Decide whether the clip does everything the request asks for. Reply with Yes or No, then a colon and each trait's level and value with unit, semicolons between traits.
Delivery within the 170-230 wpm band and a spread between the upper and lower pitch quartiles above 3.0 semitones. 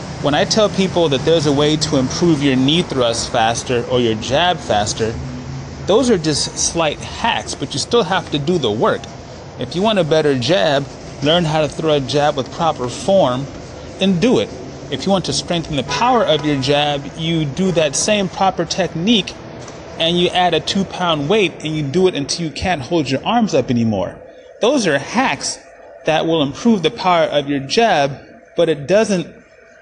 Yes: average, 195 wpm; average, 4.5 semitones